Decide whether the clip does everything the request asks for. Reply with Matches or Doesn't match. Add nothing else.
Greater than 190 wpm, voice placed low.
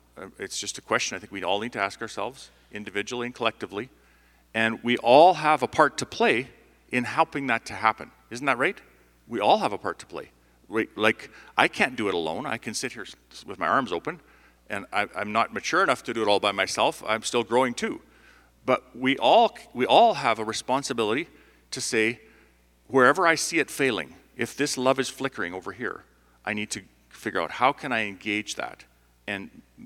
Matches